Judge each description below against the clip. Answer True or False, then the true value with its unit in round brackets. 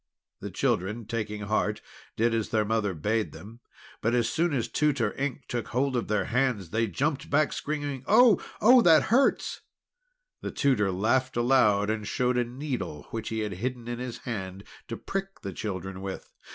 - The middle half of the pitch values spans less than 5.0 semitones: True (4.3 semitones)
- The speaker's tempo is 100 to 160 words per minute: False (180 wpm)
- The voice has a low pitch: True (115 Hz)